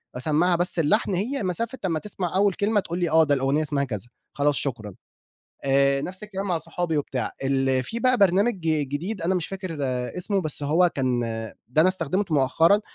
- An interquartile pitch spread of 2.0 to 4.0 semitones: No, average, 5.1 semitones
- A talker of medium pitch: Yes, medium, 165 Hz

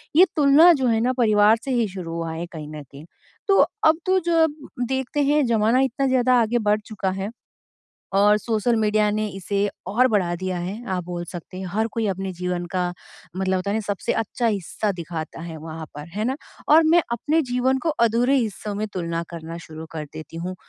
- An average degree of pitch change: No, wide, 5.9 semitones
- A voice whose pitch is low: No, high, 210 Hz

